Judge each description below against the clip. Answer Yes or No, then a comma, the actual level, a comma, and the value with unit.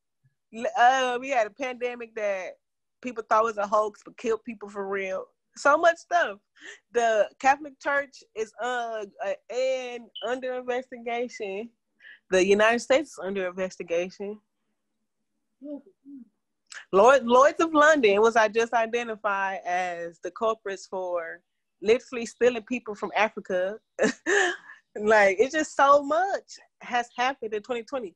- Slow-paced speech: Yes, slow, 130 wpm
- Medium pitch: No, high, 235 Hz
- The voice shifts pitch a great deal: No, average, 4.2 semitones